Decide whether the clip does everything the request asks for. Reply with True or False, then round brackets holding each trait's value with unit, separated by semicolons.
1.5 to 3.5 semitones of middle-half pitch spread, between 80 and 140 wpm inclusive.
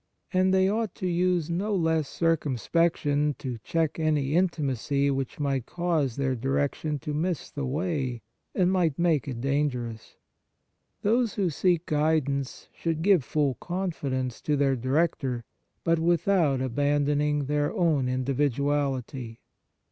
False (3.9 semitones; 135 wpm)